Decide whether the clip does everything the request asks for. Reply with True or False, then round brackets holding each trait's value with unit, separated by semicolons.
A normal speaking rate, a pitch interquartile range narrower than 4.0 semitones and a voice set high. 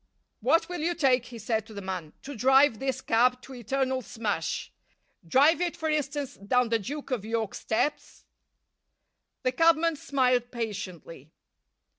False (150 wpm; 4.5 semitones; 250 Hz)